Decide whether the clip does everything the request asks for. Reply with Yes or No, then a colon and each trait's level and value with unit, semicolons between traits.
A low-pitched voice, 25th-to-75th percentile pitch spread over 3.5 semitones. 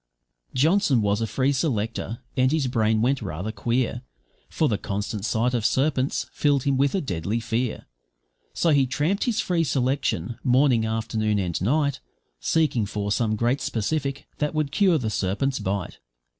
Yes: low, 125 Hz; average, 4.7 semitones